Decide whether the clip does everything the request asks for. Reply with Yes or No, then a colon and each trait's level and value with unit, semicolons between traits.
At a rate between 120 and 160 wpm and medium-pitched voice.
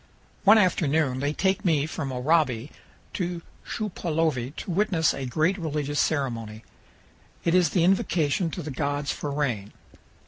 Yes: average, 140 wpm; medium, 155 Hz